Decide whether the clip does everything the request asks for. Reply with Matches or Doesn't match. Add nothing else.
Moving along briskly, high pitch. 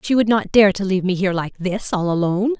Matches